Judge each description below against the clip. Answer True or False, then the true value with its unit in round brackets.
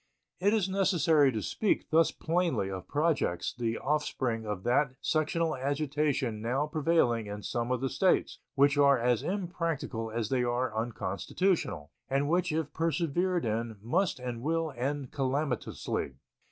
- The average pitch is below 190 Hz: True (140 Hz)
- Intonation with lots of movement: True (5.7 semitones)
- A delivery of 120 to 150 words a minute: True (145 wpm)